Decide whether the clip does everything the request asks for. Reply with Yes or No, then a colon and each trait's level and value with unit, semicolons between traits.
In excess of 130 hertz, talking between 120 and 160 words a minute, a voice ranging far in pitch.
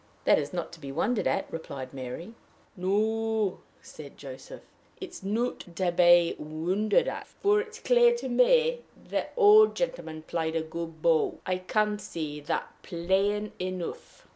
Yes: medium, 185 Hz; average, 155 wpm; wide, 5.7 semitones